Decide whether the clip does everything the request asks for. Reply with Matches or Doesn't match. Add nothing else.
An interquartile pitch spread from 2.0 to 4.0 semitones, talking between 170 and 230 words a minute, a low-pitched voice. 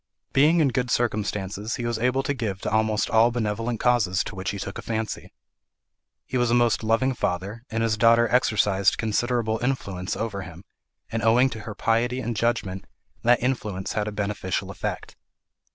Matches